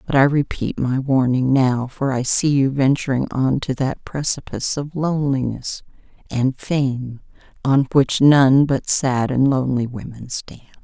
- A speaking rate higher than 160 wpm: No, average, 155 wpm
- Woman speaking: Yes, female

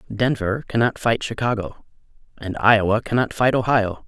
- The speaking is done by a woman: No, male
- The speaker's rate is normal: No, slow, 130 wpm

